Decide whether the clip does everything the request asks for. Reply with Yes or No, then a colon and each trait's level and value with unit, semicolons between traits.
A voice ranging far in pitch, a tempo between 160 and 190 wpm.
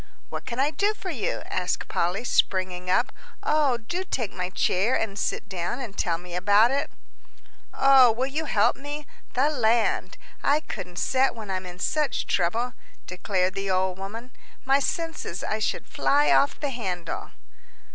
Yes: wide, 6.7 semitones; average, 165 wpm